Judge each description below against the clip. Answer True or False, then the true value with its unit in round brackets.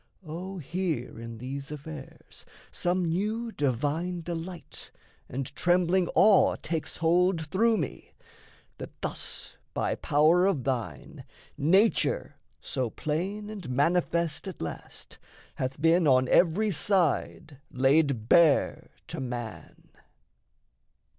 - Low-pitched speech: False (165 Hz)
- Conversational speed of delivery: False (110 wpm)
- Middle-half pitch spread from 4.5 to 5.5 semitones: True (4.9 semitones)